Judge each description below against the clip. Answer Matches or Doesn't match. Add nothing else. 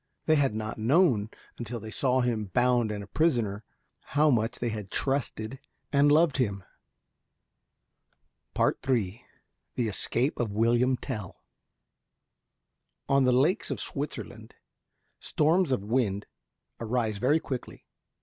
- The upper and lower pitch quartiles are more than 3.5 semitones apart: Matches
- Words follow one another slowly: Matches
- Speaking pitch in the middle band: Doesn't match